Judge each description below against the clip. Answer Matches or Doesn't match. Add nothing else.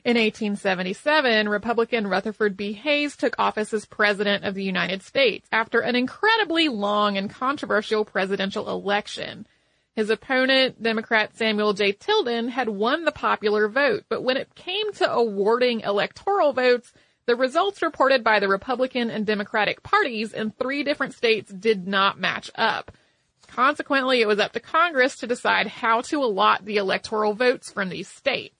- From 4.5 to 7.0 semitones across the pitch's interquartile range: Doesn't match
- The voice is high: Matches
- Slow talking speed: Doesn't match